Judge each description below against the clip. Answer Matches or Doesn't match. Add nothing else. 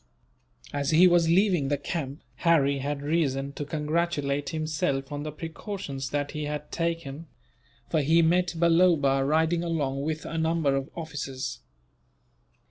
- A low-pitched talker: Doesn't match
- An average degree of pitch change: Matches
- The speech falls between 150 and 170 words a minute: Doesn't match